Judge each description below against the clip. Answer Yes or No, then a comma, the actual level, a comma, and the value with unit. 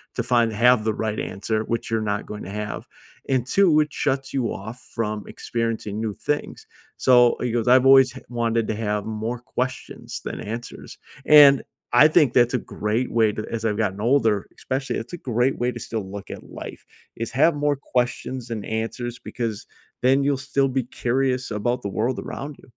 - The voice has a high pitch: No, low, 120 Hz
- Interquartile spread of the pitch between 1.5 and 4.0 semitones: Yes, average, 2.9 semitones